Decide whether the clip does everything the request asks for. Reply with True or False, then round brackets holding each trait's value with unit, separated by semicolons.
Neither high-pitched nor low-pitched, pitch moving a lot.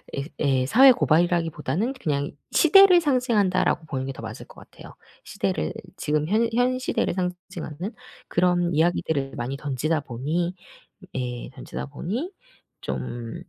True (170 Hz; 7.4 semitones)